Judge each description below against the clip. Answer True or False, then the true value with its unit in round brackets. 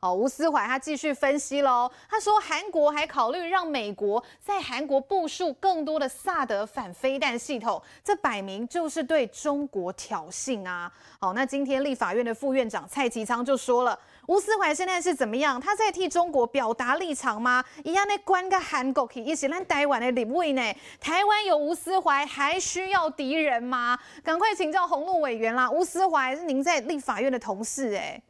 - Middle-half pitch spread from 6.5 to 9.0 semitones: False (5.5 semitones)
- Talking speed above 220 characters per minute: True (280 characters per minute)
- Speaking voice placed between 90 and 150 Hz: False (285 Hz)